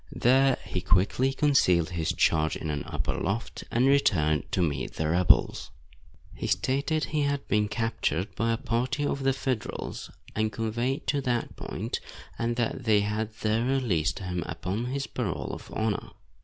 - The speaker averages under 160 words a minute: No, average, 165 wpm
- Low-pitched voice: Yes, low, 115 Hz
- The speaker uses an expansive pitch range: Yes, wide, 6.3 semitones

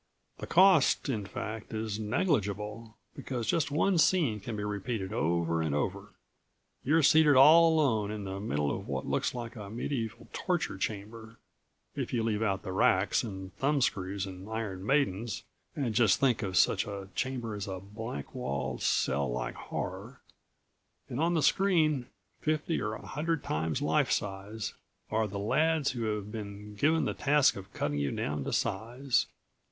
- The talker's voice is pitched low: Yes, low, 110 Hz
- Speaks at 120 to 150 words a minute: No, average, 165 wpm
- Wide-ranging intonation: Yes, wide, 5.8 semitones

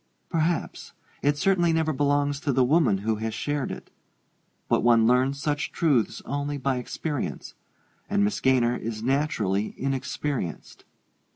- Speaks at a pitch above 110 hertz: Yes, medium, 140 Hz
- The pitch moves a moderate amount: Yes, average, 3.7 semitones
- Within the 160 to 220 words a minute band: No, slow, 135 wpm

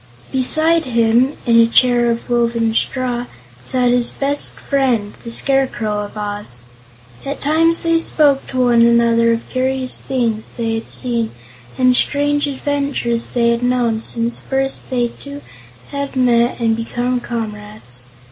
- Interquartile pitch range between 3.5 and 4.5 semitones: No, narrow, 2.6 semitones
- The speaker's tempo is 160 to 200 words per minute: No, average, 145 wpm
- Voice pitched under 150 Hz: No, high, 245 Hz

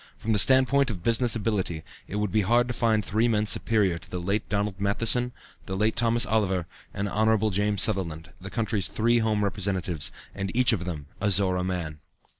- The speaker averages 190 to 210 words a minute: Yes, average, 195 wpm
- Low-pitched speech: Yes, low, 105 Hz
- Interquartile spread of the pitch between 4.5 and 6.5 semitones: No, average, 3.1 semitones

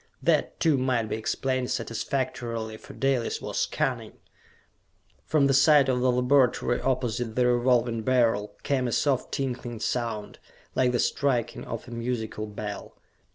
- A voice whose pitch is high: No, low, 125 Hz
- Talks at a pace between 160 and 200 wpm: No, average, 145 wpm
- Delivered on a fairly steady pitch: Yes, narrow, 2.1 semitones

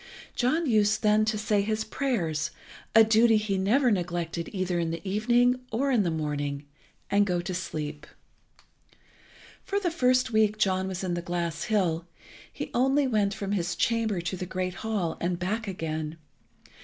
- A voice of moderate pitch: No, high, 200 Hz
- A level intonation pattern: No, average, 4.2 semitones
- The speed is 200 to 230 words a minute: No, average, 165 wpm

